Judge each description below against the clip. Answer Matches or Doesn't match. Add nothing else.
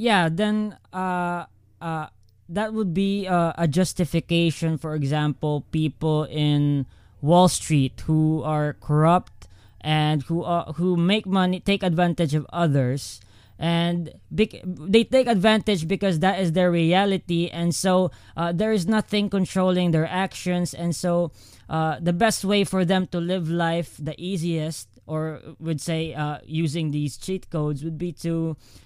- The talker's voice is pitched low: Doesn't match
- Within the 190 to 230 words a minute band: Doesn't match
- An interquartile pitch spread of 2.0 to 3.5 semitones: Matches